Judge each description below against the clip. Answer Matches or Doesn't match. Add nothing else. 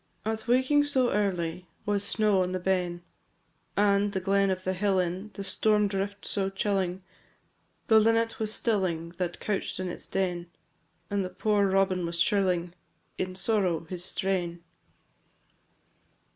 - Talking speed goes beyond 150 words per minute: Doesn't match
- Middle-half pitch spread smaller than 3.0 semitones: Matches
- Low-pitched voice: Doesn't match